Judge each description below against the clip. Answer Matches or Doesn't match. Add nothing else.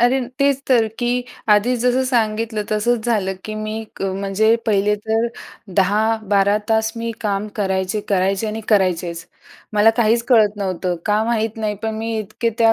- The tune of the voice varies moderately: Doesn't match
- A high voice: Matches